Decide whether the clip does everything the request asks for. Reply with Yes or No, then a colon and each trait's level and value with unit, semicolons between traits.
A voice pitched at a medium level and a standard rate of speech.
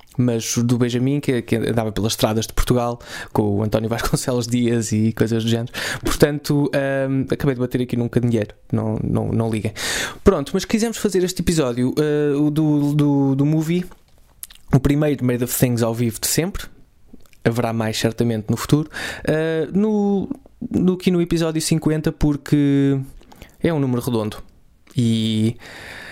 No: low, 125 Hz; average, 160 wpm